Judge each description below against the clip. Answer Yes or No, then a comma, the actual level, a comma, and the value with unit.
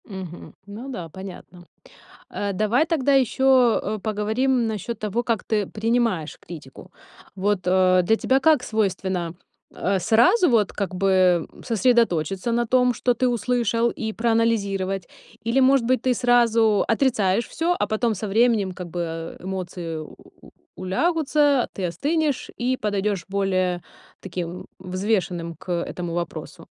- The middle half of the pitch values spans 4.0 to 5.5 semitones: Yes, average, 4.7 semitones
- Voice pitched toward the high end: Yes, high, 210 Hz